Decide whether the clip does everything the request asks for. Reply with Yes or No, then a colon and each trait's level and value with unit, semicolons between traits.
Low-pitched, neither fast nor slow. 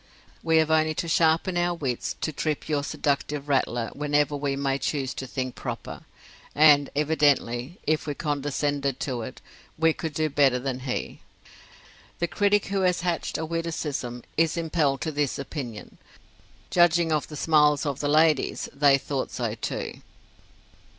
No: medium, 150 Hz; average, 155 wpm